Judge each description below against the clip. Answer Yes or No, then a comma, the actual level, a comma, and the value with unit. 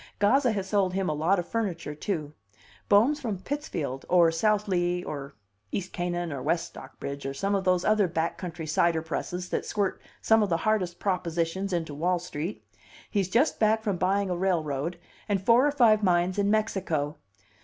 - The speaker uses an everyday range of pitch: Yes, average, 3.7 semitones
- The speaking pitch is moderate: Yes, medium, 180 Hz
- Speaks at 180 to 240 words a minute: Yes, average, 185 wpm